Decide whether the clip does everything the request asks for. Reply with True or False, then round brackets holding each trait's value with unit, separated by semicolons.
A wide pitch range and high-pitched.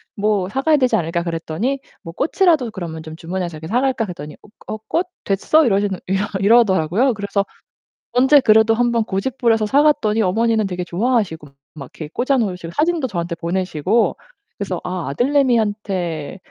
True (5.7 semitones; 205 Hz)